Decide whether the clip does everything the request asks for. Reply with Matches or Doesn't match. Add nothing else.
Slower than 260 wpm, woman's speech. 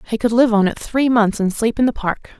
Doesn't match